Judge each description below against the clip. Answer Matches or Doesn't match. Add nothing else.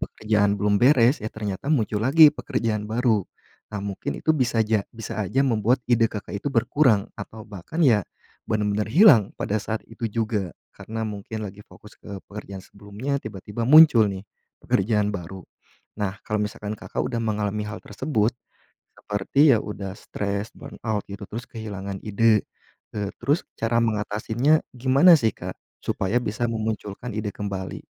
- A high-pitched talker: Doesn't match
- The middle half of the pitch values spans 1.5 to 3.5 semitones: Matches